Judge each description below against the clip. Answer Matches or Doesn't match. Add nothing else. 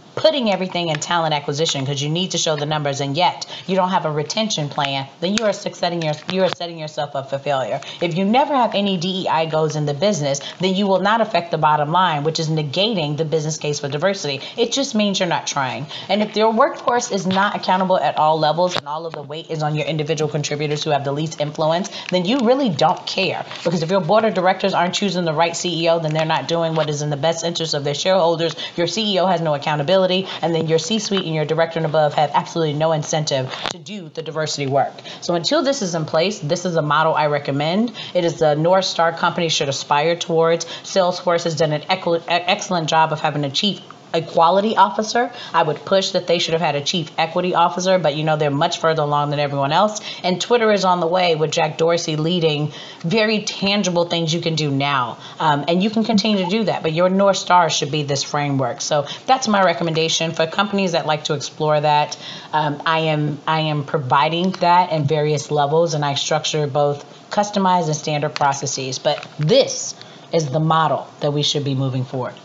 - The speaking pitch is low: Doesn't match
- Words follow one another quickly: Matches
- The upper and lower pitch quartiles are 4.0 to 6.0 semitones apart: Doesn't match